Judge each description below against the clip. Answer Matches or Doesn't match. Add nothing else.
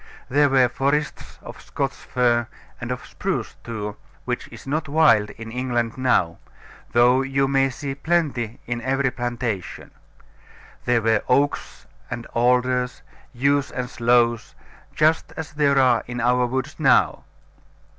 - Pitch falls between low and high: Doesn't match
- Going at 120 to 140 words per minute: Matches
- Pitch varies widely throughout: Doesn't match